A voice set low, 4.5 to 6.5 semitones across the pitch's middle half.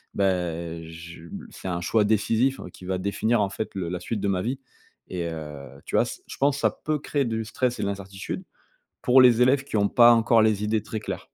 Yes: low, 105 Hz; average, 4.8 semitones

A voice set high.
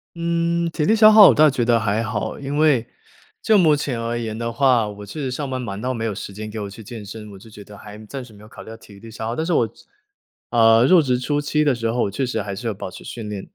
No: low, 115 Hz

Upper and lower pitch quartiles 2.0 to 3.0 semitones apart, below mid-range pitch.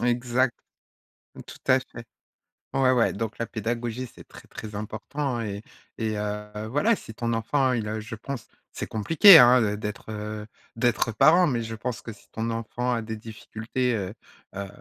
Yes: narrow, 2.5 semitones; low, 115 Hz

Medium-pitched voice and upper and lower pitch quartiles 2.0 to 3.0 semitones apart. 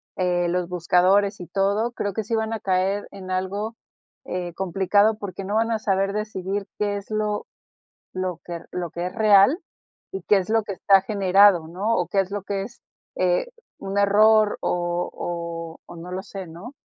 No: high, 195 Hz; narrow, 2.6 semitones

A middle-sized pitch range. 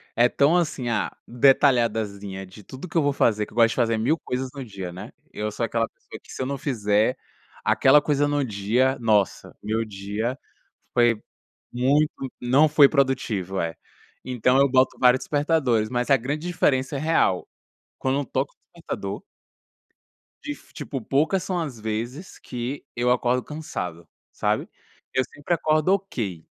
Yes: average, 4.5 semitones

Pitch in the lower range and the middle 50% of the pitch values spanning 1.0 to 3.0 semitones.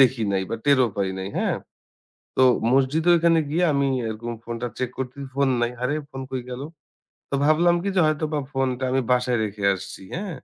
No: low, 130 Hz; average, 4.2 semitones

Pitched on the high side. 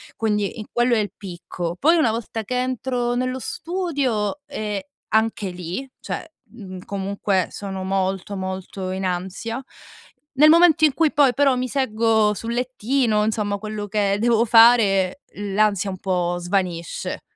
Yes: high, 215 Hz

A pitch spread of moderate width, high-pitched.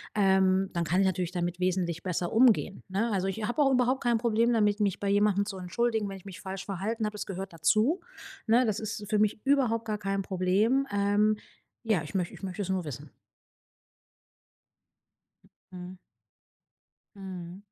Yes: average, 3.0 semitones; high, 200 Hz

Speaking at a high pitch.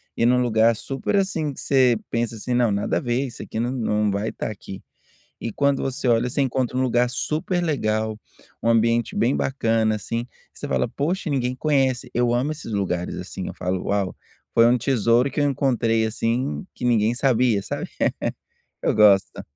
No: low, 120 Hz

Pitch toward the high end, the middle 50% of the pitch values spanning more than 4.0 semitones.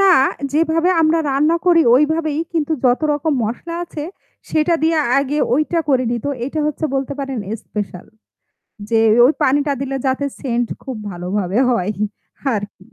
Yes: very high, 280 Hz; average, 4.7 semitones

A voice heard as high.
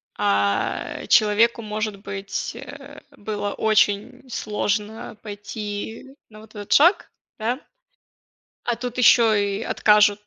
Yes: high, 215 Hz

